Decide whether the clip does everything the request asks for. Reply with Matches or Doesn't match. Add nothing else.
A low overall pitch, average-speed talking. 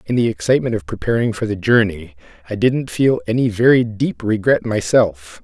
Matches